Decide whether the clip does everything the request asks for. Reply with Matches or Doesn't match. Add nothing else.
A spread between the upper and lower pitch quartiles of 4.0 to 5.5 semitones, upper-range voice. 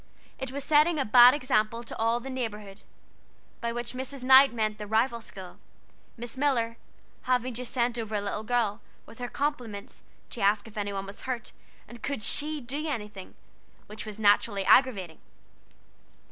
Doesn't match